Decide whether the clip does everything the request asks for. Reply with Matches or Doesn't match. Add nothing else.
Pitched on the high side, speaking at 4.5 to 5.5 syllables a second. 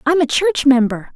Matches